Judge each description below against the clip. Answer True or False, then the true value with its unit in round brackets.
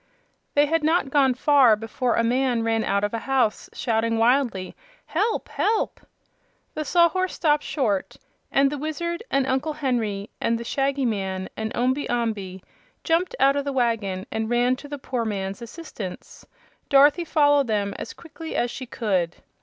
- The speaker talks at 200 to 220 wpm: False (165 wpm)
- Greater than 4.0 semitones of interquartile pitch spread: True (4.7 semitones)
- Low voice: False (255 Hz)